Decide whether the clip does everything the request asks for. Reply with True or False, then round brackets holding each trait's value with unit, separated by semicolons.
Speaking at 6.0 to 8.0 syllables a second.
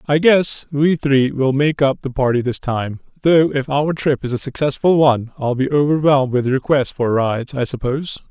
False (5.1 syllables/s)